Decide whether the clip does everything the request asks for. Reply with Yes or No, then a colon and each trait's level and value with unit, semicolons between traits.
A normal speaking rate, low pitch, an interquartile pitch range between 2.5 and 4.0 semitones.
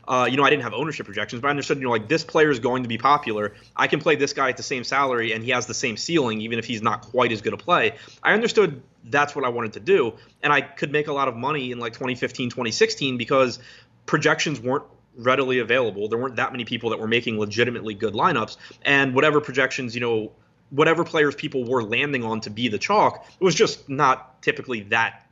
No: fast, 240 wpm; low, 130 Hz; average, 3.3 semitones